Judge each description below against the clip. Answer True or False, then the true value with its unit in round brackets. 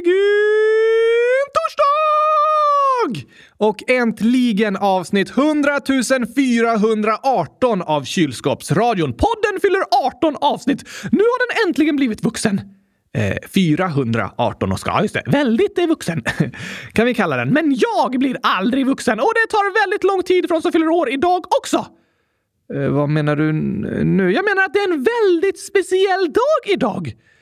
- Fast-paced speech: False (145 wpm)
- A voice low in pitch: False (275 Hz)